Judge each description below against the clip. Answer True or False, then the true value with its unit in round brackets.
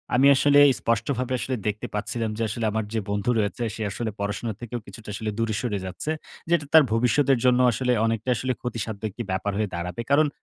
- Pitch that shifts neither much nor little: True (3.2 semitones)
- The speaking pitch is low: True (115 Hz)